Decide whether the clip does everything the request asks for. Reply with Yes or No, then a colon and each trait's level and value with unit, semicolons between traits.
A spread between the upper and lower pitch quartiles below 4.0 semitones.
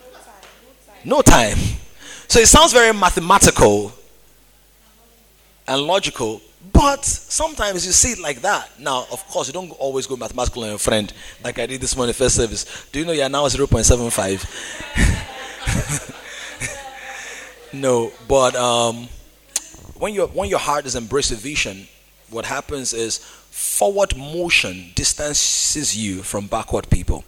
No: average, 5.2 semitones